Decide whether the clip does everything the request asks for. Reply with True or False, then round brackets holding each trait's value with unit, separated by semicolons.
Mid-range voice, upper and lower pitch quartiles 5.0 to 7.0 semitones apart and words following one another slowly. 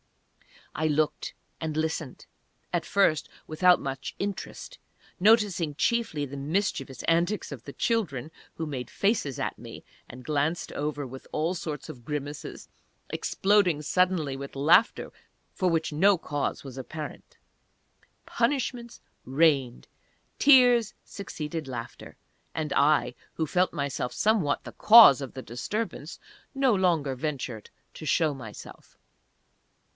True (155 Hz; 5.4 semitones; 125 wpm)